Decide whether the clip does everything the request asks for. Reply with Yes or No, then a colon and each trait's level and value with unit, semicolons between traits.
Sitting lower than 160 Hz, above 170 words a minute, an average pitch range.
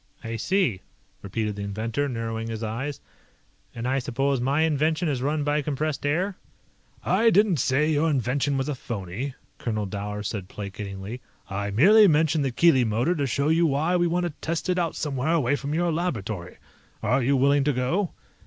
No: medium, 140 Hz; average, 180 wpm; wide, 5.8 semitones